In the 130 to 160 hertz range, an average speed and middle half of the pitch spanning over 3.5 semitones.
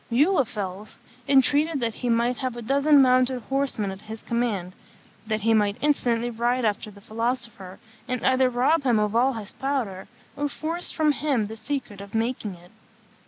No: high, 240 Hz; average, 170 wpm; average, 3.9 semitones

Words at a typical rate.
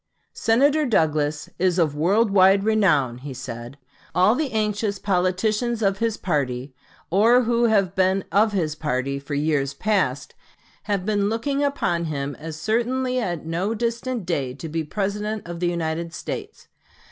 Yes: average, 160 wpm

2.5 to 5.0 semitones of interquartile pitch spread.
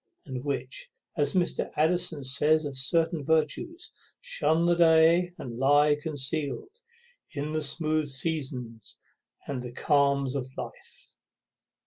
Yes: average, 3.0 semitones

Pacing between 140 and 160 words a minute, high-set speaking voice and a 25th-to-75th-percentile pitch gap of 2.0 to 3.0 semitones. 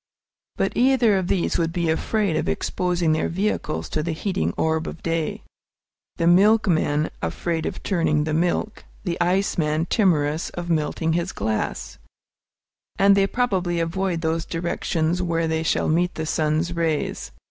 No: average, 155 wpm; medium, 170 Hz; narrow, 2.5 semitones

